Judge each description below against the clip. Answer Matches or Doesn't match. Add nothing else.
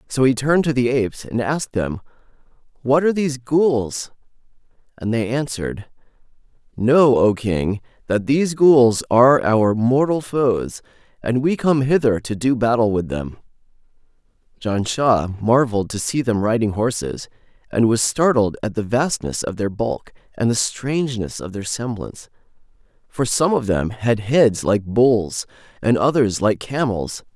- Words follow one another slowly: Doesn't match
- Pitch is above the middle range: Doesn't match